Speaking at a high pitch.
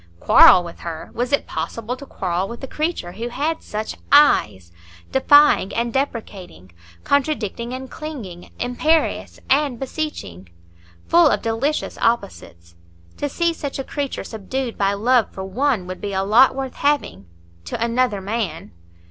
Yes: high, 230 Hz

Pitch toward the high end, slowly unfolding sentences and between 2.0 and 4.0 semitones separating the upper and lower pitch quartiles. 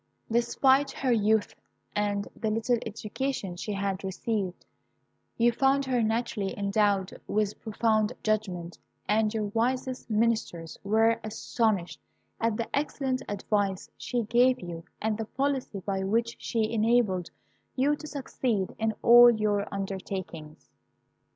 Yes: high, 220 Hz; slow, 125 wpm; average, 3.0 semitones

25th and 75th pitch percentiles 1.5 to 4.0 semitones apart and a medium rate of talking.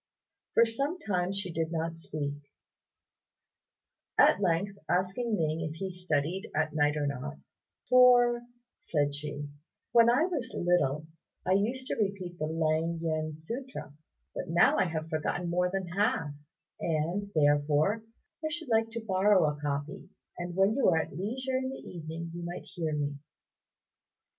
No: average, 5.1 semitones; average, 155 wpm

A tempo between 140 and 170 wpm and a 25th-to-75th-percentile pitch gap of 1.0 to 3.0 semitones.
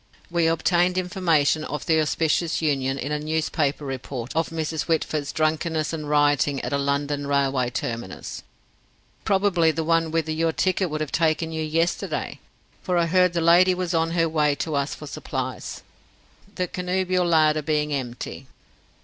Yes: average, 160 wpm; narrow, 2.5 semitones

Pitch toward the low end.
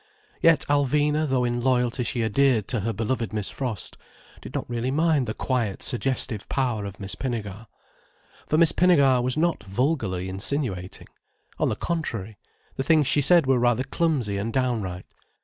Yes: low, 125 Hz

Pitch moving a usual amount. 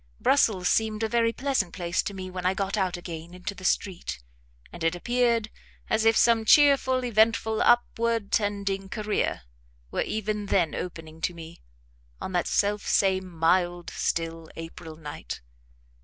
Yes: average, 4.2 semitones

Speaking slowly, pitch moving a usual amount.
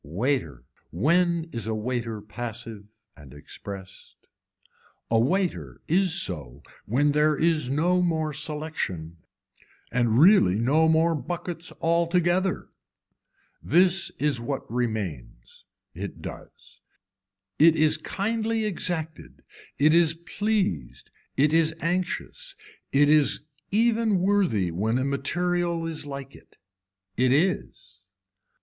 No: slow, 110 wpm; wide, 6.9 semitones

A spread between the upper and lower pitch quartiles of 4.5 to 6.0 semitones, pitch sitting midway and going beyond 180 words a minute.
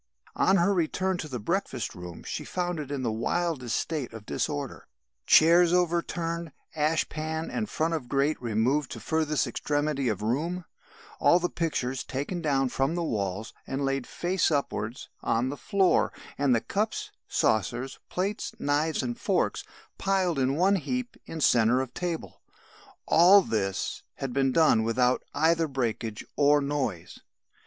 No: average, 5.2 semitones; medium, 145 Hz; average, 155 wpm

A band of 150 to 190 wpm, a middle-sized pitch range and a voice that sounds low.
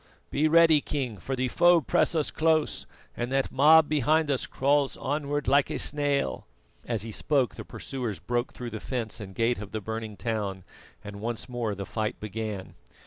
Yes: average, 185 wpm; average, 4.8 semitones; low, 125 Hz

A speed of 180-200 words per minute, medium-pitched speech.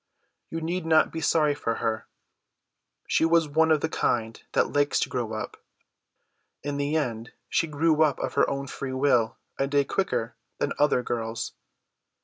No: average, 170 wpm; medium, 145 Hz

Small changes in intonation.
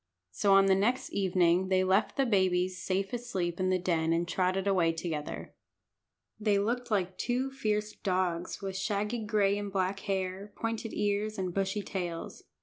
Yes: narrow, 2.3 semitones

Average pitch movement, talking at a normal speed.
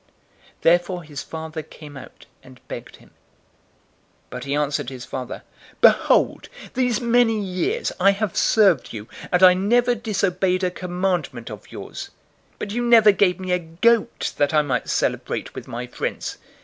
No: wide, 6.2 semitones; average, 160 wpm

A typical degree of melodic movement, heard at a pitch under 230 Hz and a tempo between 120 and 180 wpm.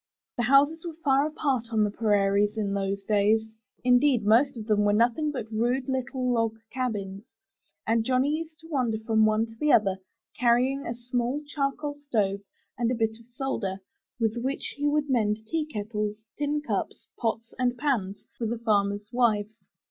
No: average, 4.1 semitones; high, 235 Hz; average, 170 wpm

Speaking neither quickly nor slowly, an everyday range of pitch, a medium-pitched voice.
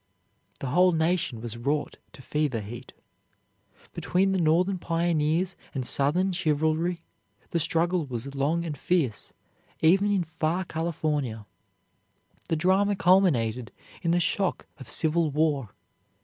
No: slow, 125 wpm; average, 4.1 semitones; medium, 160 Hz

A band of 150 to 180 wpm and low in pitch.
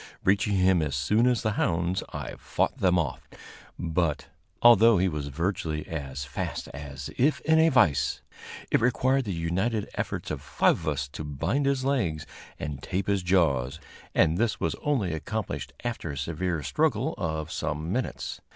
Yes: average, 170 wpm; very low, 85 Hz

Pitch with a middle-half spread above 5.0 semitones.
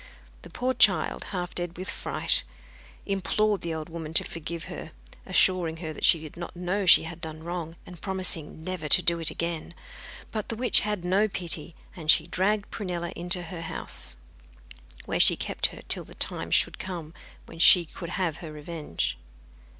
No: narrow, 2.4 semitones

